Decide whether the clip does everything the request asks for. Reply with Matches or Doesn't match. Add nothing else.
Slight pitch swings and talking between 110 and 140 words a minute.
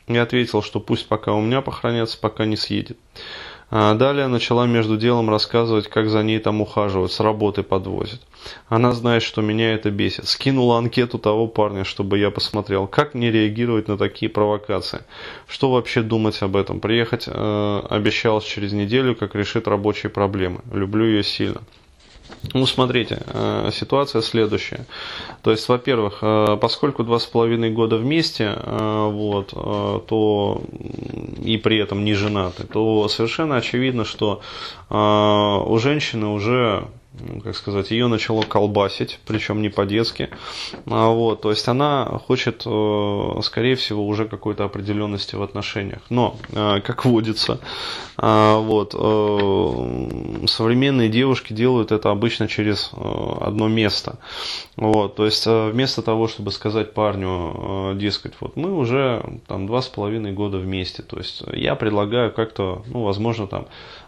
Matches